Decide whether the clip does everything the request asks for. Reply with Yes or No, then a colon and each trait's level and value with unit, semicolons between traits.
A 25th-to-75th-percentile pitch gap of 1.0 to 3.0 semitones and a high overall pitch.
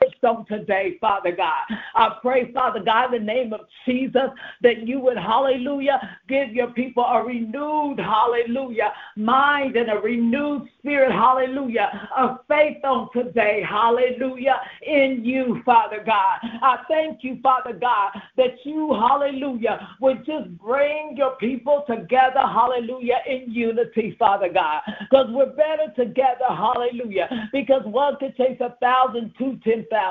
Yes: narrow, 2.6 semitones; very high, 250 Hz